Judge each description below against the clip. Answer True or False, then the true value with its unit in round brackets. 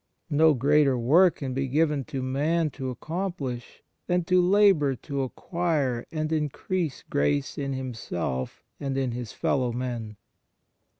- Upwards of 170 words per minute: False (135 wpm)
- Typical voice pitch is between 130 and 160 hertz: True (140 Hz)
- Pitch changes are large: False (4.2 semitones)